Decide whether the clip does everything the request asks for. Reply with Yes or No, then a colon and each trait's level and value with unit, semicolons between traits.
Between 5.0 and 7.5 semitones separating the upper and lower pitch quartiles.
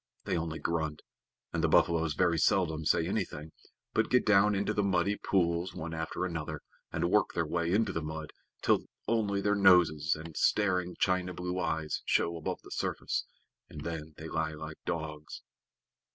No: average, 2.8 semitones